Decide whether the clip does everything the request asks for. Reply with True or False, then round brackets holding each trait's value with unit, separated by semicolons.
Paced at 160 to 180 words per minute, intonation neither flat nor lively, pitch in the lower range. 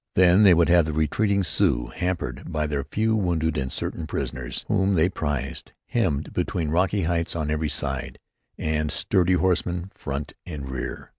True (165 wpm; 3.6 semitones; 80 Hz)